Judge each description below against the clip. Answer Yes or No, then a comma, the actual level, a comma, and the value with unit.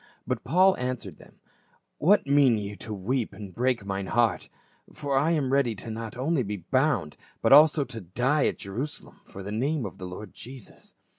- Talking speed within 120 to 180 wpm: No, average, 195 wpm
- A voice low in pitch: Yes, low, 125 Hz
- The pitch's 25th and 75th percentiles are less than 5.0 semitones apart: No, average, 5.3 semitones